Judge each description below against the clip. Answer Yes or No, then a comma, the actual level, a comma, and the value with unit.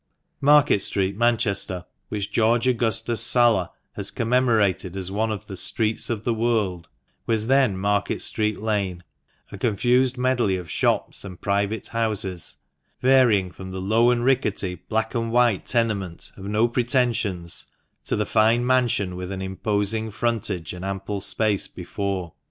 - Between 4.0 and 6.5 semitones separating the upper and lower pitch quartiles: No, average, 3.5 semitones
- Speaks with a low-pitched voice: Yes, low, 110 Hz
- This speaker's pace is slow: No, average, 150 wpm